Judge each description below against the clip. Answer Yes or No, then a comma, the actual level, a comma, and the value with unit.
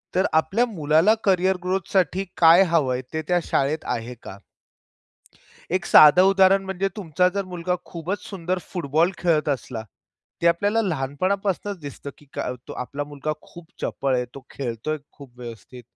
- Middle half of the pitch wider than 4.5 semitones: Yes, average, 4.9 semitones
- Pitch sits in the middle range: Yes, medium, 170 Hz